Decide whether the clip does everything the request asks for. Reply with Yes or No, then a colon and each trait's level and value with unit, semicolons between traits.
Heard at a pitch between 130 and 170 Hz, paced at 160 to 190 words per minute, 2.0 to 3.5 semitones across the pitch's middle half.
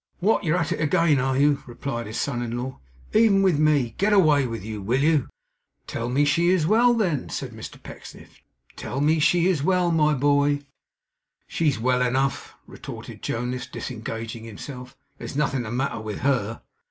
No: medium, 140 Hz; average, 175 wpm; average, 4.9 semitones